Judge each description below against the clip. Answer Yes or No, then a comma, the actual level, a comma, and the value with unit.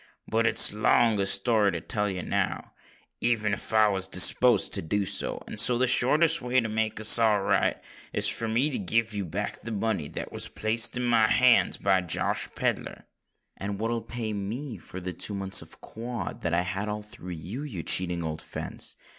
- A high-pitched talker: No, low, 105 Hz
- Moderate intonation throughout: Yes, average, 3.2 semitones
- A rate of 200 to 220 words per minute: Yes, fast, 205 wpm